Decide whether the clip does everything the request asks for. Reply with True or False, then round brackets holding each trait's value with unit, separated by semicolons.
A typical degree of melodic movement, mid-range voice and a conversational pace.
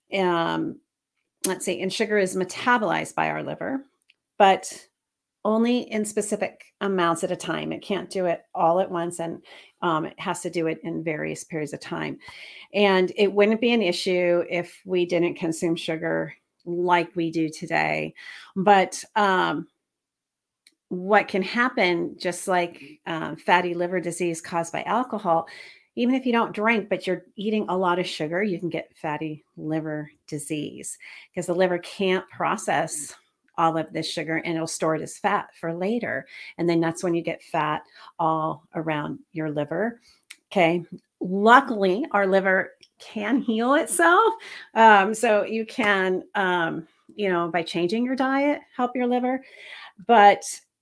True (4.0 semitones; 180 Hz; 160 wpm)